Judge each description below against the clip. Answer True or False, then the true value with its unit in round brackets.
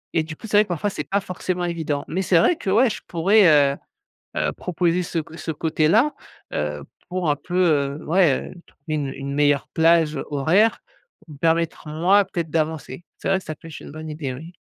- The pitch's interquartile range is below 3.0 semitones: False (3.3 semitones)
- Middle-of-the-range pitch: True (165 Hz)